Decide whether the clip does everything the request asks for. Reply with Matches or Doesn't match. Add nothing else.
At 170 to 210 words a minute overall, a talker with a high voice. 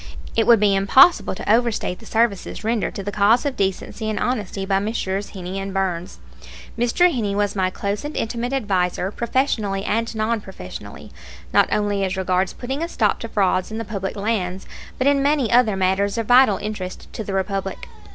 Matches